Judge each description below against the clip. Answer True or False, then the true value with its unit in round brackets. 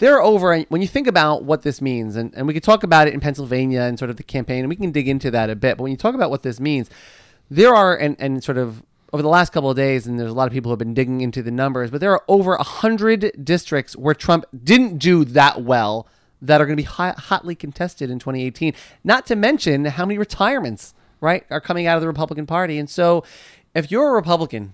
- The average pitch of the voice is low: False (150 Hz)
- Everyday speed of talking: False (255 wpm)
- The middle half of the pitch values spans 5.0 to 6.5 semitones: True (5.3 semitones)